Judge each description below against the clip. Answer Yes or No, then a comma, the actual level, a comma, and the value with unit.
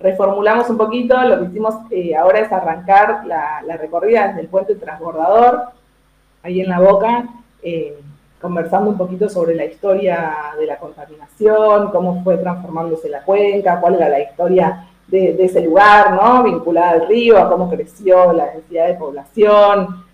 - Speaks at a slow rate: No, average, 165 wpm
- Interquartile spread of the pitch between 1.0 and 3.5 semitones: No, average, 3.9 semitones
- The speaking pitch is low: No, medium, 185 Hz